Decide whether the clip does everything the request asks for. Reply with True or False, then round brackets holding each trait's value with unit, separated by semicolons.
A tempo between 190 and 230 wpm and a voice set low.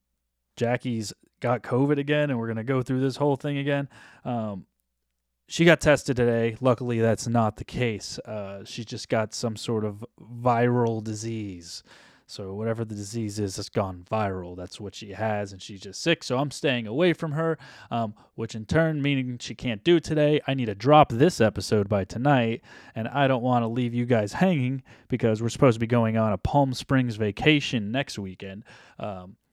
True (195 wpm; 115 Hz)